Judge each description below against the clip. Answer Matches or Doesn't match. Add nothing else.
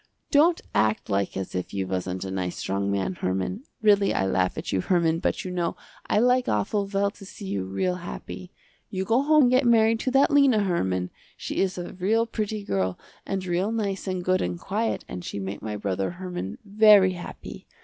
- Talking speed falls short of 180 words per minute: Doesn't match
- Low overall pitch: Doesn't match